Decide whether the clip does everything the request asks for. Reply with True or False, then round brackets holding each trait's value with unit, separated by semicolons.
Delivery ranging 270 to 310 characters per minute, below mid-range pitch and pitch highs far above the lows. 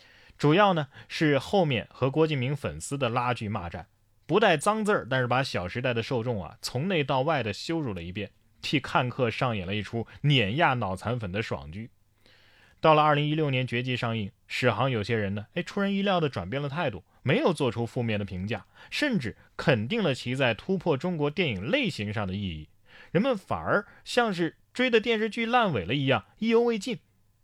True (295 characters per minute; 125 Hz; 7.4 semitones)